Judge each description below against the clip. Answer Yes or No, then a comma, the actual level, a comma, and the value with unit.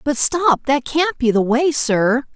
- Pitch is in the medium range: No, very high, 265 Hz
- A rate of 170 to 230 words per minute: Yes, fast, 205 wpm